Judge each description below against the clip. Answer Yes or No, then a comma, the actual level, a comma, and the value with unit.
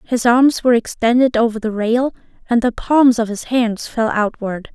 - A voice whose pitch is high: Yes, high, 235 Hz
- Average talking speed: Yes, average, 190 wpm